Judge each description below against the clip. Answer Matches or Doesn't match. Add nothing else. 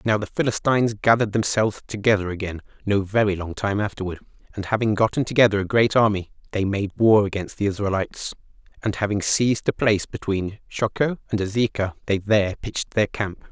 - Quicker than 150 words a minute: Matches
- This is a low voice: Matches